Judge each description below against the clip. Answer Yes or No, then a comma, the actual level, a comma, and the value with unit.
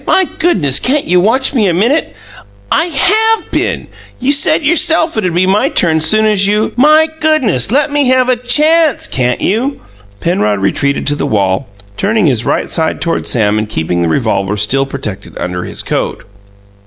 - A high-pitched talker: Yes, high, 200 Hz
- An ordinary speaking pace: Yes, average, 180 wpm